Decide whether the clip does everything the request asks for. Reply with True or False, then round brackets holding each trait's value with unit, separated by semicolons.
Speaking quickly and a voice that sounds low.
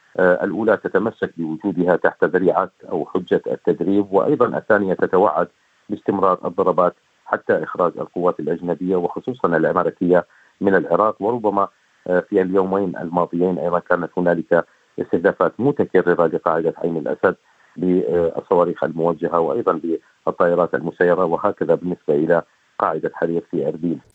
False (110 wpm; 90 Hz)